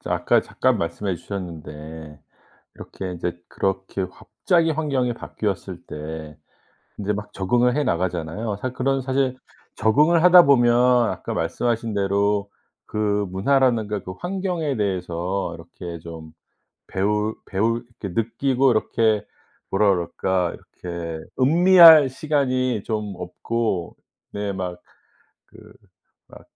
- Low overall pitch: Yes, low, 105 Hz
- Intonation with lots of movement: Yes, wide, 6.1 semitones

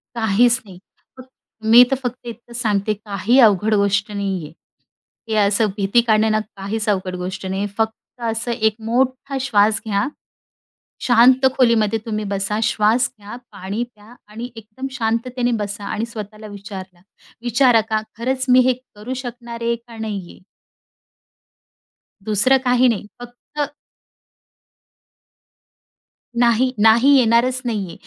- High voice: Yes, high, 225 Hz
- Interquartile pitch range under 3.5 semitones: Yes, average, 2.8 semitones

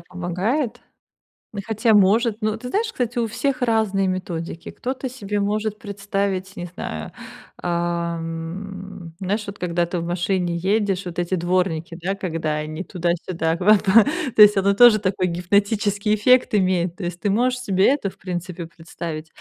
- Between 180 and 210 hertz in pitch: Yes, high, 190 Hz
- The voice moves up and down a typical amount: Yes, average, 3.5 semitones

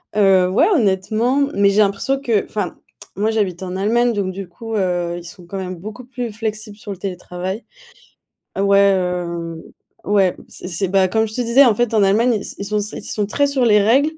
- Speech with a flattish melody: No, average, 3.2 semitones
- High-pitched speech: Yes, high, 200 Hz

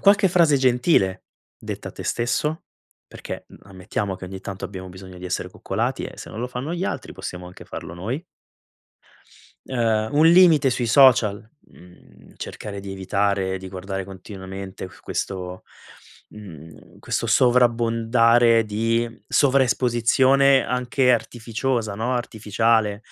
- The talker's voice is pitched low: Yes, low, 115 Hz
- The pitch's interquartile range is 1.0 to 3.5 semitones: No, average, 4.6 semitones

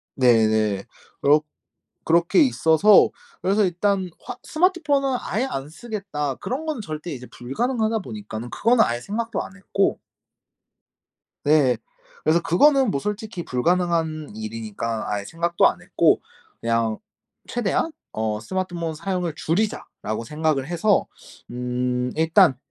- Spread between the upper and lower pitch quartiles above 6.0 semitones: Yes, wide, 8.8 semitones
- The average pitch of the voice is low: No, medium, 165 Hz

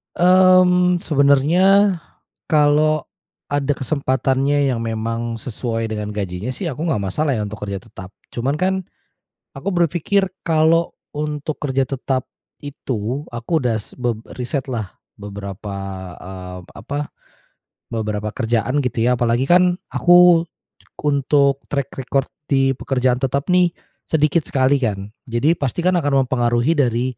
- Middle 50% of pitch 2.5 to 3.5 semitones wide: No, average, 4.9 semitones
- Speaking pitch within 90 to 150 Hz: Yes, low, 135 Hz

